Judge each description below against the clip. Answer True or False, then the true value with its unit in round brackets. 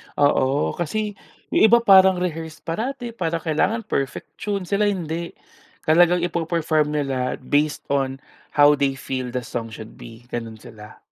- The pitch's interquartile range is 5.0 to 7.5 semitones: True (5.3 semitones)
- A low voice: False (160 Hz)